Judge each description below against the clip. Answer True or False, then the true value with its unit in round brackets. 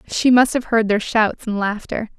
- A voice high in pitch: True (220 Hz)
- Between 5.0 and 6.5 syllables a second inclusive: False (4.6 syllables/s)